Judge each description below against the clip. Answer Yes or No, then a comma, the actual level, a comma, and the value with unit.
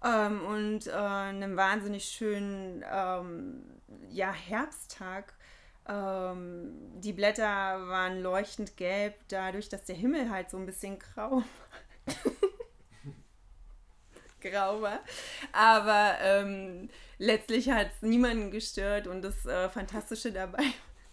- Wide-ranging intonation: No, average, 2.9 semitones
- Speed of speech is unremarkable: No, slow, 110 wpm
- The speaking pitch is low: No, high, 205 Hz